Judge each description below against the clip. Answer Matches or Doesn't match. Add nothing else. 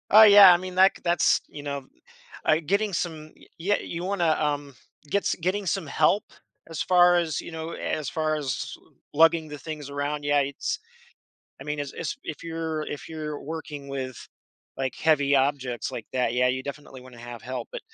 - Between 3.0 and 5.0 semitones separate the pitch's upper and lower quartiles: Matches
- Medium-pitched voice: Matches